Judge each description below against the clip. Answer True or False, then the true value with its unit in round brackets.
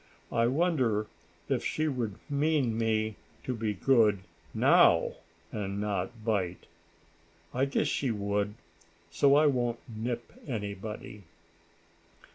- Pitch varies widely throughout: False (4.1 semitones)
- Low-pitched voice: True (115 Hz)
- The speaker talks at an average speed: False (110 wpm)